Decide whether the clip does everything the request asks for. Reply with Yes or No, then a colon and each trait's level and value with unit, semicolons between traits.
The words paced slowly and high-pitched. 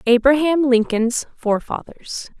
Yes: slow, 75 wpm; very high, 255 Hz